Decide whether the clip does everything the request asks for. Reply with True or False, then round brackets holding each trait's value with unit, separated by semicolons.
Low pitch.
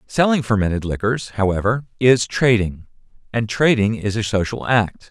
True (110 Hz)